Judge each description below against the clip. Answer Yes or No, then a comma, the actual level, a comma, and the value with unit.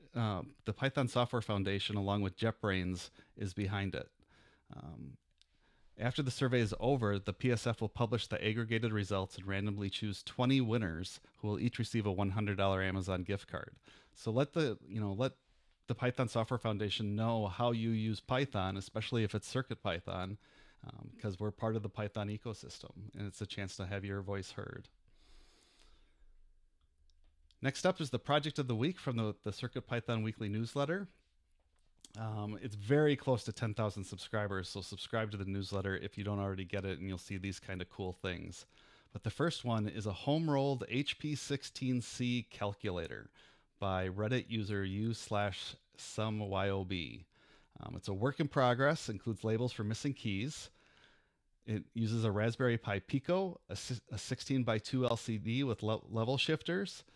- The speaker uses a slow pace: No, average, 165 wpm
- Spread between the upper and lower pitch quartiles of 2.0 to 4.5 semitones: Yes, average, 3.9 semitones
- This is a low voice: Yes, low, 110 Hz